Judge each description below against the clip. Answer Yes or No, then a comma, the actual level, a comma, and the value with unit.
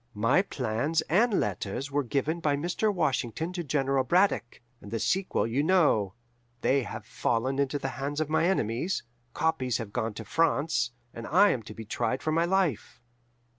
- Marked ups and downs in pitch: Yes, wide, 5.8 semitones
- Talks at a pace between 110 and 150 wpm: No, average, 175 wpm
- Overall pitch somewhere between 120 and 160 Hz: Yes, medium, 140 Hz